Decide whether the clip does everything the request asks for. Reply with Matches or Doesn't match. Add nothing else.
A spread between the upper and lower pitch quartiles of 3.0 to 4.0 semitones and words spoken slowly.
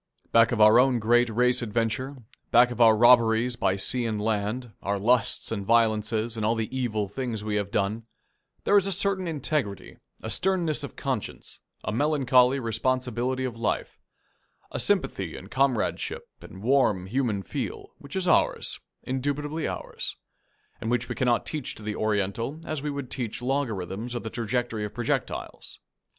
Doesn't match